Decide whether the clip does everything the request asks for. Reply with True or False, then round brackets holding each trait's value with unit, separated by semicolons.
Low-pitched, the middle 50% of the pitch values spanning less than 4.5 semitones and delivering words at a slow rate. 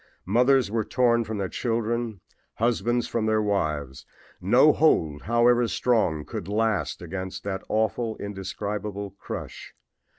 True (110 Hz; 3.4 semitones; 125 wpm)